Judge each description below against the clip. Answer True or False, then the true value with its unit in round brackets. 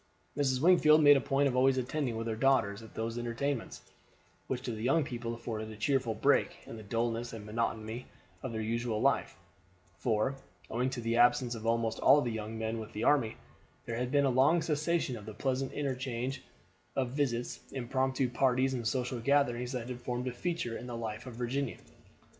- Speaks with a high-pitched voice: False (125 Hz)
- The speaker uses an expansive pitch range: False (2.8 semitones)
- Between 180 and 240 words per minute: True (195 wpm)